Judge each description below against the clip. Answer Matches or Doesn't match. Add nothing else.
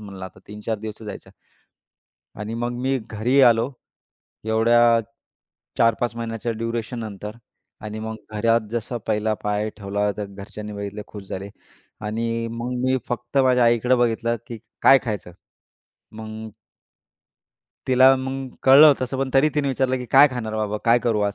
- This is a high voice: Doesn't match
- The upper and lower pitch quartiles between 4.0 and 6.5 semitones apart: Doesn't match